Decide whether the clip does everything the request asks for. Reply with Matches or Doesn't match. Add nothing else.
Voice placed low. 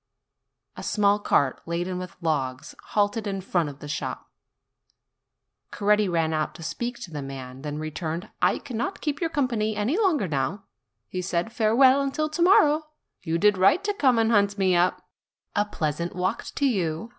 Doesn't match